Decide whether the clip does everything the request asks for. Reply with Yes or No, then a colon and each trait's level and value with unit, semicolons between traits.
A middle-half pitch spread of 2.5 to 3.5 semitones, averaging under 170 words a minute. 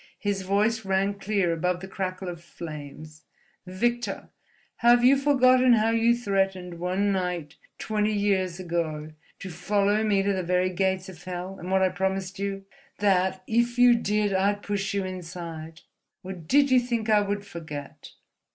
Yes: average, 2.8 semitones; average, 160 wpm